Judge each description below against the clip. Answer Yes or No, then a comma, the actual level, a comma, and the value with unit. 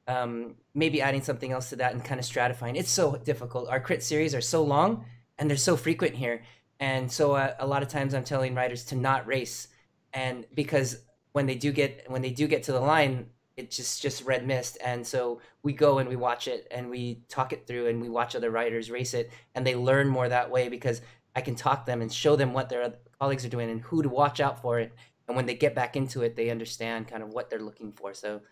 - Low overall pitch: Yes, low, 125 Hz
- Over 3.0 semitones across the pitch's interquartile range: No, narrow, 2.5 semitones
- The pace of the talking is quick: Yes, fast, 250 wpm